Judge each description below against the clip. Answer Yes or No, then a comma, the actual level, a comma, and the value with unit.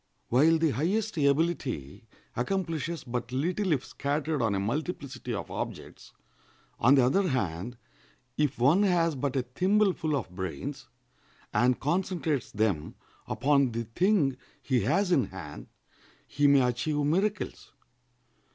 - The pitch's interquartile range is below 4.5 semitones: No, wide, 5.6 semitones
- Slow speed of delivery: Yes, slow, 130 wpm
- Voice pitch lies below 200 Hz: Yes, medium, 140 Hz